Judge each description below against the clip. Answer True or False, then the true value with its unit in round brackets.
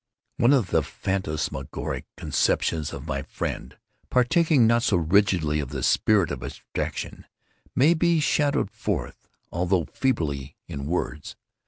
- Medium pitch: False (95 Hz)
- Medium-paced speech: False (130 wpm)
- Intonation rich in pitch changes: True (8.6 semitones)